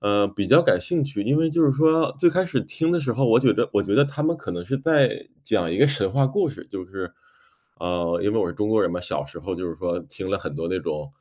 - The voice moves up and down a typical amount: No, wide, 8.4 semitones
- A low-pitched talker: Yes, low, 115 Hz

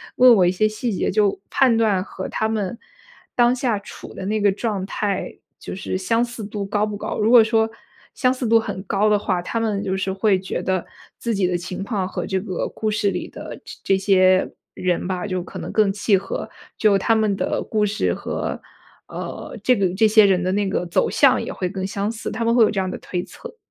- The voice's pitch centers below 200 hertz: No, high, 205 Hz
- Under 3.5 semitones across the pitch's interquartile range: Yes, average, 2.7 semitones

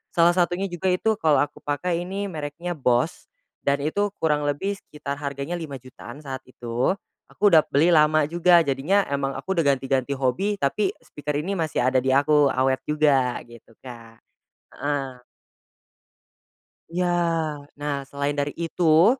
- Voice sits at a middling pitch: Yes, medium, 145 Hz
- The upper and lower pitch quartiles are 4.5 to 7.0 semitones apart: No, average, 4.1 semitones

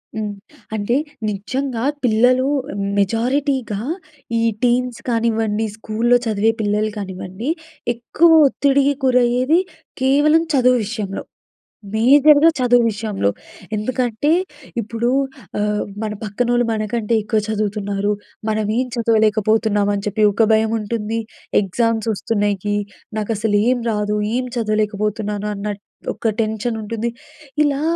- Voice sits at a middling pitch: No, high, 220 Hz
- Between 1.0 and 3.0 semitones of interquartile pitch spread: Yes, average, 2.7 semitones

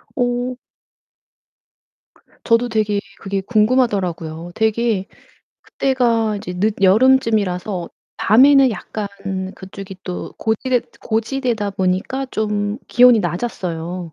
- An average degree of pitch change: Yes, average, 4.3 semitones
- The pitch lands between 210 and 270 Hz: Yes, high, 215 Hz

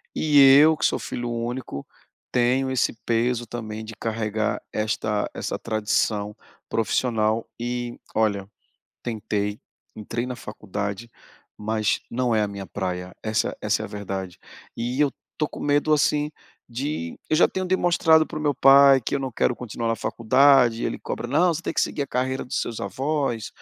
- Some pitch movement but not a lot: Yes, average, 4.1 semitones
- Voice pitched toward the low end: Yes, low, 115 Hz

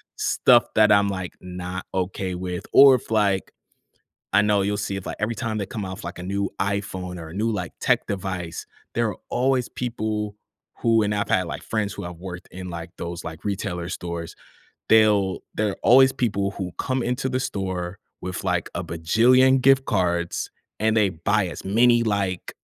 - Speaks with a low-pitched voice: Yes, low, 100 Hz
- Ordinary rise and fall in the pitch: Yes, average, 3.3 semitones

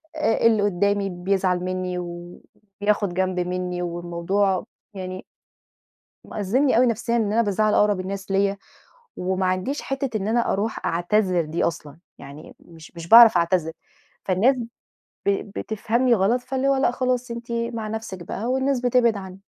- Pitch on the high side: Yes, high, 200 Hz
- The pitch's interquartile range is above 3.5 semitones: Yes, average, 4.2 semitones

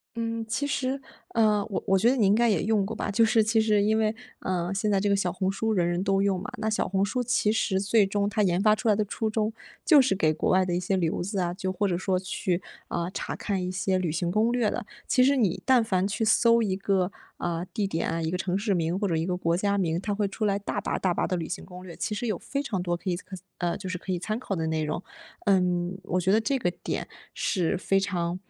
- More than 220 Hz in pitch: No, high, 195 Hz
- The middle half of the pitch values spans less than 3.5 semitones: Yes, average, 3.1 semitones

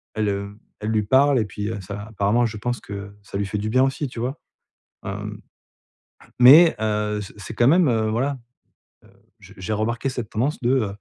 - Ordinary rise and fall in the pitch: Yes, average, 3.6 semitones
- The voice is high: No, low, 110 Hz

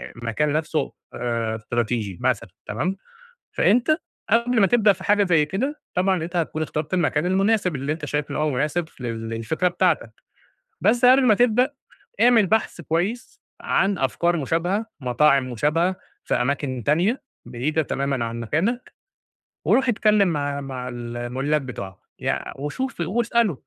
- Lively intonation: Yes, wide, 7.7 semitones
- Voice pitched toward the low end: No, medium, 155 Hz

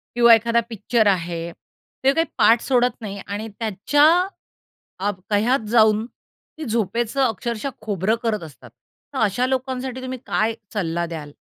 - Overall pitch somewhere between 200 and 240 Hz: Yes, high, 220 Hz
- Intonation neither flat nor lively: Yes, average, 3.6 semitones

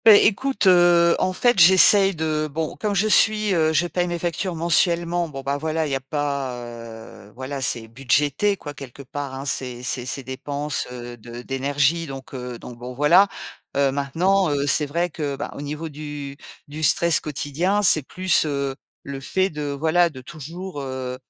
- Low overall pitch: No, medium, 145 Hz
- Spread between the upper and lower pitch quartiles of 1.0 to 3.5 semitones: No, average, 4.2 semitones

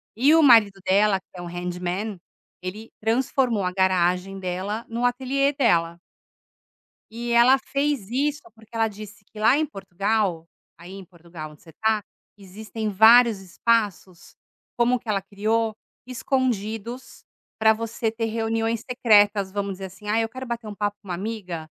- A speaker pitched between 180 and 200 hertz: No, high, 215 Hz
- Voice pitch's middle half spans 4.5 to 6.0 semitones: No, average, 3.5 semitones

